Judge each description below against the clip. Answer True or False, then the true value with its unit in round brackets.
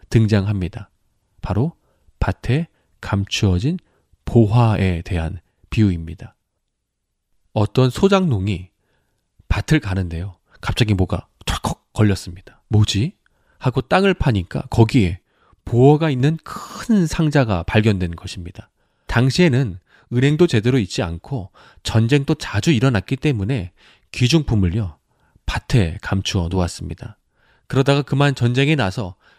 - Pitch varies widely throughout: True (6.2 semitones)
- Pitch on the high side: False (110 Hz)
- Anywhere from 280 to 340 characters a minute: False (260 characters per minute)